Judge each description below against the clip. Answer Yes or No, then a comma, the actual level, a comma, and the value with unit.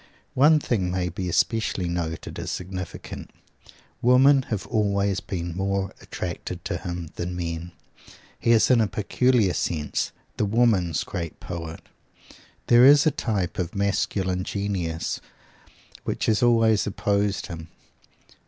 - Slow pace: Yes, slow, 130 wpm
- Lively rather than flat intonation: No, average, 4.2 semitones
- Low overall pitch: Yes, low, 100 Hz